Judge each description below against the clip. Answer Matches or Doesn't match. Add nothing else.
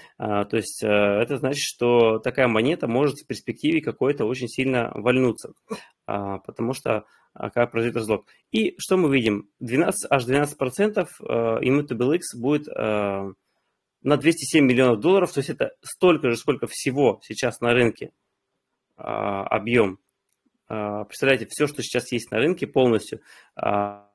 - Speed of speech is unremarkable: Matches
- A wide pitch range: Doesn't match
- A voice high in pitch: Doesn't match